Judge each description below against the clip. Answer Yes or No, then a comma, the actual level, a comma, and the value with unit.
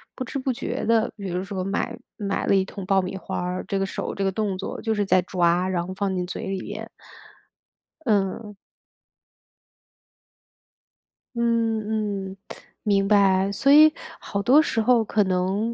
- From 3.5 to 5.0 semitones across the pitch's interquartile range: No, average, 2.8 semitones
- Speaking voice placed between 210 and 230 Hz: No, high, 200 Hz